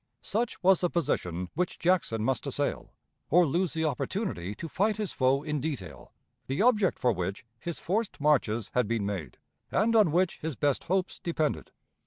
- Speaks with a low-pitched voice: No, medium, 155 Hz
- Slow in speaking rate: No, average, 175 wpm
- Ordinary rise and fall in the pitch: No, wide, 8.1 semitones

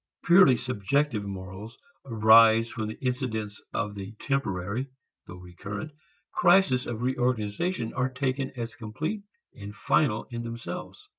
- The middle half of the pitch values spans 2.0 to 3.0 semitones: No, average, 3.7 semitones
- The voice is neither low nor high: No, low, 115 Hz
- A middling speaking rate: No, slow, 125 wpm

